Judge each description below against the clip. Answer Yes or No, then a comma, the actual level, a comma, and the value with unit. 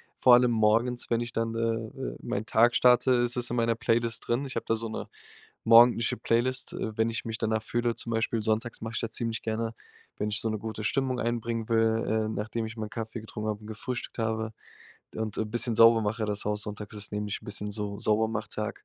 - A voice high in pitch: No, low, 115 Hz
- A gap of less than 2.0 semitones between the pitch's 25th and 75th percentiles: Yes, narrow, 1.3 semitones